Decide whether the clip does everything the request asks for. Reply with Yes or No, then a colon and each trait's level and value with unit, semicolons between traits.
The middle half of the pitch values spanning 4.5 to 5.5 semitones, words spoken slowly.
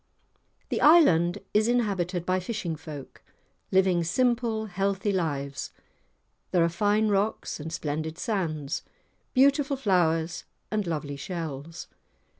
Yes: average, 4.9 semitones; slow, 110 wpm